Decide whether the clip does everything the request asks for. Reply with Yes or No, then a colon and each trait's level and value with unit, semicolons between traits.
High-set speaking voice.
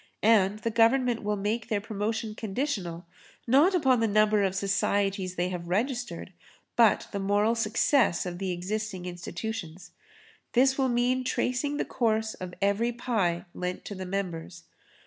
Yes: high, 210 Hz